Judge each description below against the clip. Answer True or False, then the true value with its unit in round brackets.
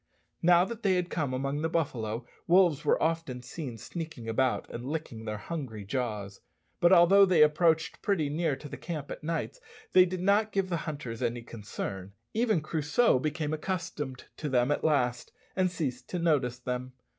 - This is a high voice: False (150 Hz)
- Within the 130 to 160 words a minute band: False (180 wpm)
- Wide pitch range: True (5.7 semitones)